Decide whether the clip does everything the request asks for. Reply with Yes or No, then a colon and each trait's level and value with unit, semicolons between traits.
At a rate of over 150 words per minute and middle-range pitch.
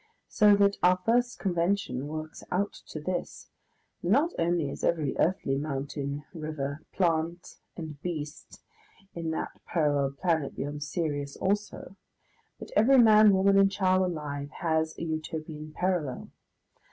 No: slow, 135 wpm; medium, 165 Hz